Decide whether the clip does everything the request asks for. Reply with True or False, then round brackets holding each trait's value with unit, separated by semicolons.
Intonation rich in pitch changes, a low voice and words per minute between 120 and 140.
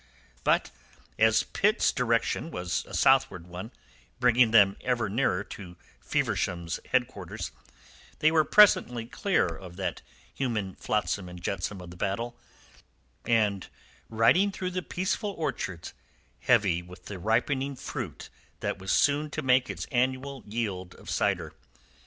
True (5.7 semitones; 115 Hz; 135 wpm)